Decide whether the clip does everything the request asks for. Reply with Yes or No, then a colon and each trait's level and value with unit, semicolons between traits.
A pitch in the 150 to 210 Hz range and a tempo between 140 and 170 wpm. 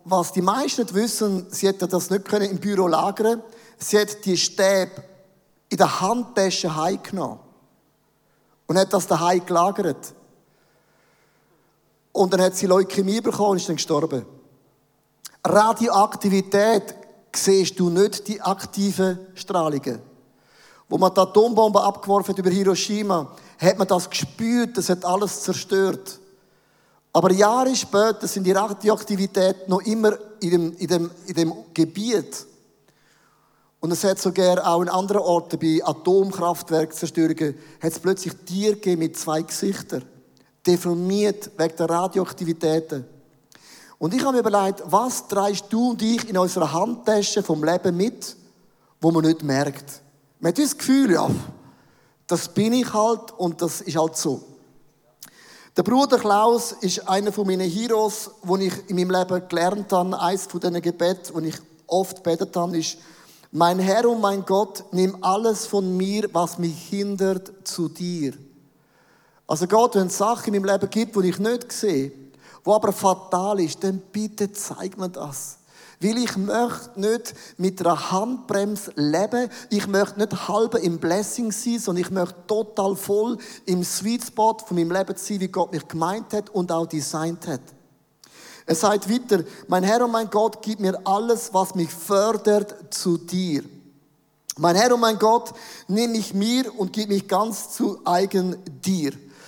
Yes: high, 190 Hz; average, 155 wpm